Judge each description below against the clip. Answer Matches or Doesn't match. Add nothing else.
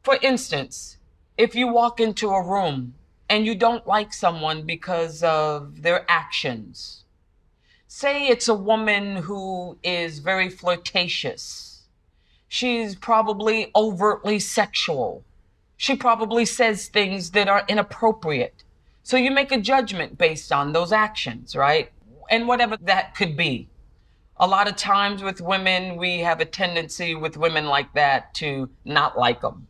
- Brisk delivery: Doesn't match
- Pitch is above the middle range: Matches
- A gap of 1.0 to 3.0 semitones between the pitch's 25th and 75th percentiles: Doesn't match